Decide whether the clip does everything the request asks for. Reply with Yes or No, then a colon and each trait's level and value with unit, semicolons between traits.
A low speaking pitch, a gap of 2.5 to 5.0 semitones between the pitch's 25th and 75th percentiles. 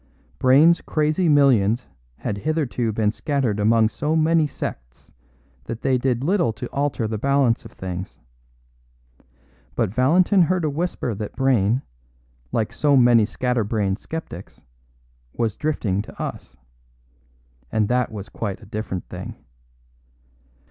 No: low, 125 Hz; wide, 5.6 semitones